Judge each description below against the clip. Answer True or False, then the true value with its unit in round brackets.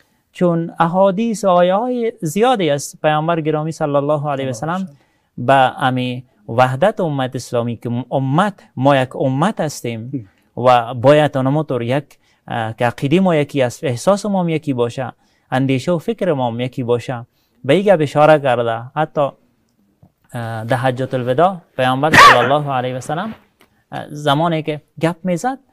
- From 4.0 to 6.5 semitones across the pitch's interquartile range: True (4.8 semitones)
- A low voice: False (145 Hz)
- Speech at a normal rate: True (150 wpm)